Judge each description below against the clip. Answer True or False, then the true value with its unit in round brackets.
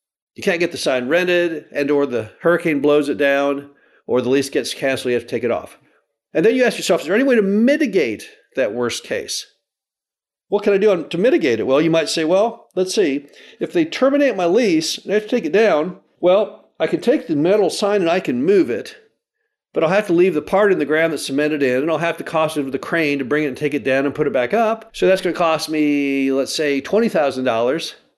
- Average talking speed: False (255 wpm)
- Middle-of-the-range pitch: True (170 Hz)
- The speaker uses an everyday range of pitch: False (7.3 semitones)